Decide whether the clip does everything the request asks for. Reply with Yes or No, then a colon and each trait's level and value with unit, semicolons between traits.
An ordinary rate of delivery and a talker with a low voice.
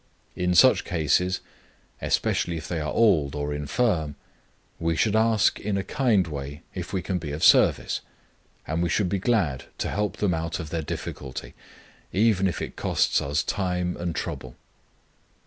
Yes: average, 165 wpm; very low, 85 Hz